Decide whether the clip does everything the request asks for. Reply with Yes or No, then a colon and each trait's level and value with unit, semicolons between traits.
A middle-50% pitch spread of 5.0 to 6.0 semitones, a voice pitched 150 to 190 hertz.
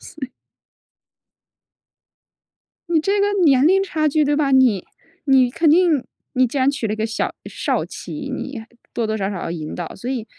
No: average, 5.3 semitones; very high, 270 Hz